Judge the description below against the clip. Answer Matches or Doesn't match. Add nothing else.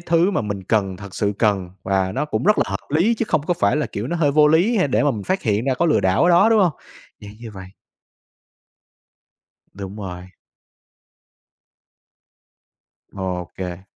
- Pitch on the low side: Matches